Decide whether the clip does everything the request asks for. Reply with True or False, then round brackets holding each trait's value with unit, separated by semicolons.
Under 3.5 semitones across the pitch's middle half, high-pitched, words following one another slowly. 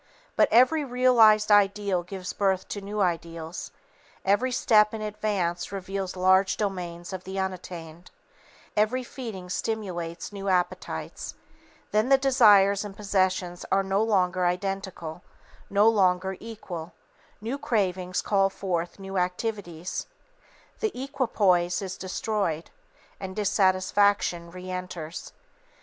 True (2.7 semitones; 195 Hz; 115 wpm)